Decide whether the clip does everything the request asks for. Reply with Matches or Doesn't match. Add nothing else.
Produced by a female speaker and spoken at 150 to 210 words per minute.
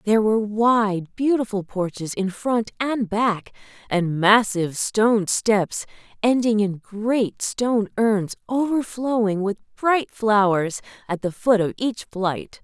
Doesn't match